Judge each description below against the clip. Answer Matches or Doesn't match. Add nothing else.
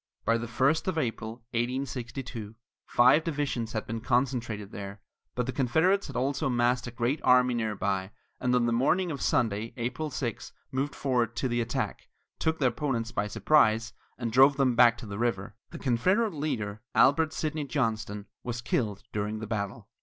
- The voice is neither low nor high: Doesn't match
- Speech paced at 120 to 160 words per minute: Doesn't match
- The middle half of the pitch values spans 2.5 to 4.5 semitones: Matches